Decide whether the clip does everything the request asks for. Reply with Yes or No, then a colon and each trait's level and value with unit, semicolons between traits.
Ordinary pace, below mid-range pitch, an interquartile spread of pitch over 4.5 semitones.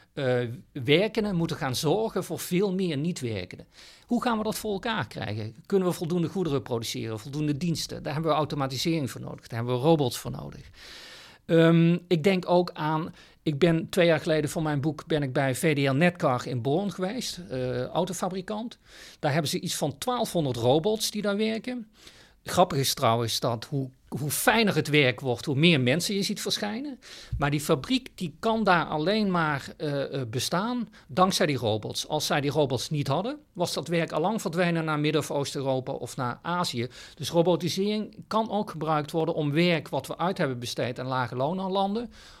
No: average, 190 wpm; medium, 160 Hz; average, 5.2 semitones